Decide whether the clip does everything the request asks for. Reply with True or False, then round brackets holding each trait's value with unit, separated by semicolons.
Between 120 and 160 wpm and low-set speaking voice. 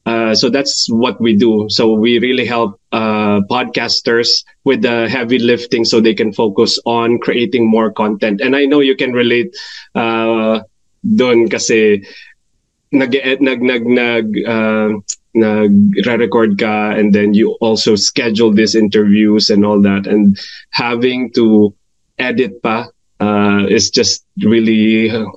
True (140 wpm; 115 Hz)